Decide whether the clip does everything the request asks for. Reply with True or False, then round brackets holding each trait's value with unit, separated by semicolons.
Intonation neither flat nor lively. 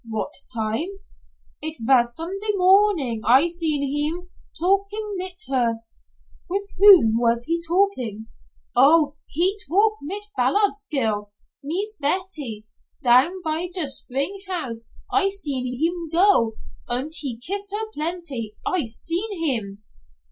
False (7.4 semitones)